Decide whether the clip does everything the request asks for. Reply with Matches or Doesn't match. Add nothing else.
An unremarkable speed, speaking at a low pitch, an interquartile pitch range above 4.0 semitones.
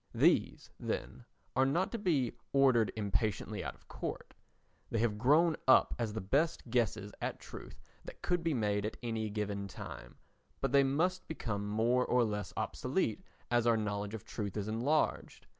Matches